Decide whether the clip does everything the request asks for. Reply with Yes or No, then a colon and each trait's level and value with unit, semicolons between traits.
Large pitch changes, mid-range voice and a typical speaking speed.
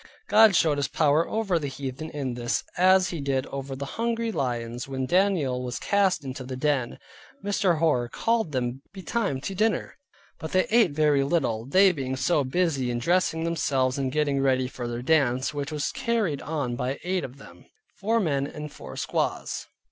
Yes: wide, 5.7 semitones; medium, 145 Hz; average, 185 wpm